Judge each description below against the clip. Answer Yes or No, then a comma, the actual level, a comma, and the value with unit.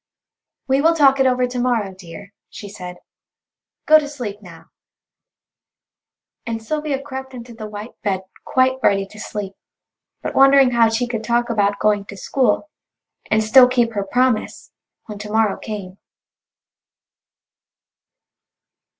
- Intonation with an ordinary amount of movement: Yes, average, 4.1 semitones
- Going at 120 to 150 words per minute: Yes, average, 140 wpm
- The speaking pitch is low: No, high, 230 Hz